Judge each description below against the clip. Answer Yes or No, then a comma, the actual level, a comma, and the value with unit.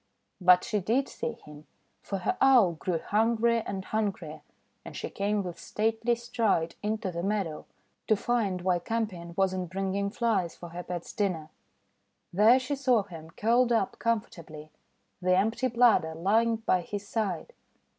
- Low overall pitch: No, high, 200 Hz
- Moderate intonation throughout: Yes, average, 4.4 semitones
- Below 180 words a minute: Yes, average, 155 wpm